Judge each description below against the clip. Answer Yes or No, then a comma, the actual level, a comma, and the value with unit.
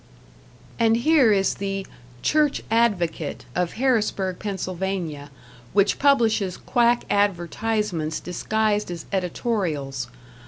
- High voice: Yes, high, 200 Hz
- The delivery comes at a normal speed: No, slow, 90 wpm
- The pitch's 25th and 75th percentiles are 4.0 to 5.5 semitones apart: Yes, average, 4.3 semitones